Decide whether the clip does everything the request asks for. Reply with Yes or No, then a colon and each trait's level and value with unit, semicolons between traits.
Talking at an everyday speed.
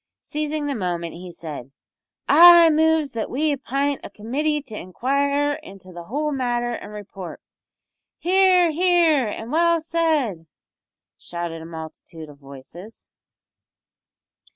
No: slow, 125 wpm